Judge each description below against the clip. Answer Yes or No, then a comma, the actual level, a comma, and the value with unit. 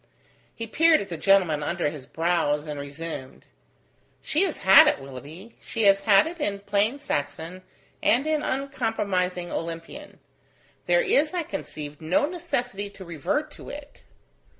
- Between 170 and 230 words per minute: No, average, 150 wpm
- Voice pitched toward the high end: Yes, high, 195 Hz